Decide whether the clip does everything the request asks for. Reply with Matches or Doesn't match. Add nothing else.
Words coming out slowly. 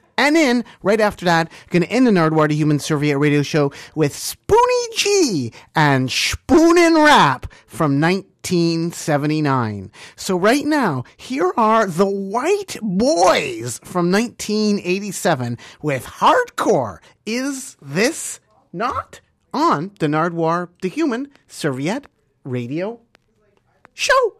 Matches